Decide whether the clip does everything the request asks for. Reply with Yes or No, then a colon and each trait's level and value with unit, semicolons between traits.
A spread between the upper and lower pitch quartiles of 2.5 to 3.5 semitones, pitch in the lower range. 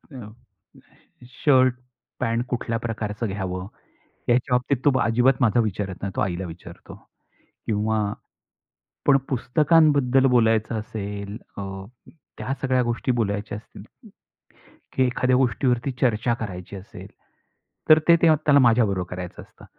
No: average, 3.9 semitones; low, 115 Hz